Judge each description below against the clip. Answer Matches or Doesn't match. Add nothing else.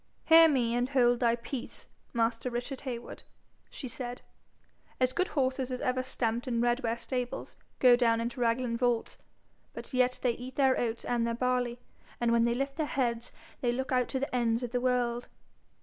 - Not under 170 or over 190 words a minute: Matches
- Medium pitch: Doesn't match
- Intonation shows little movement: Matches